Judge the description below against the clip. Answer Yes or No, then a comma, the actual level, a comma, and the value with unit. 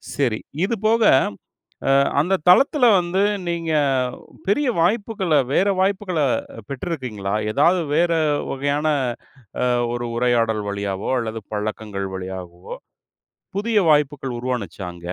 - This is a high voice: No, medium, 140 Hz